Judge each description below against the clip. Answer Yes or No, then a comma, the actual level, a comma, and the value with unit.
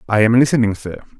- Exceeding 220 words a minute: No, average, 200 wpm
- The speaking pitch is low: Yes, low, 115 Hz